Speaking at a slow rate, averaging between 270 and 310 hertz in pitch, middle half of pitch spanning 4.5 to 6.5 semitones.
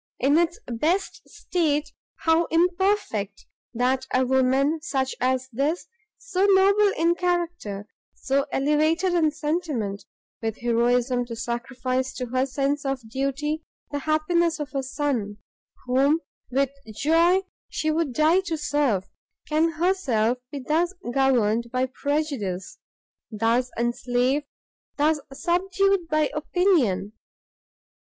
Yes: slow, 115 wpm; very high, 285 Hz; average, 4.8 semitones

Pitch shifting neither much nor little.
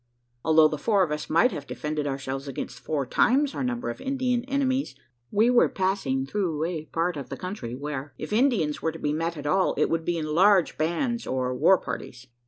No: wide, 6.2 semitones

